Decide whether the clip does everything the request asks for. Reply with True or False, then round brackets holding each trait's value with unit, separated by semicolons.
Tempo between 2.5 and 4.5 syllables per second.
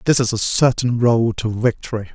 False (5.1 syllables/s)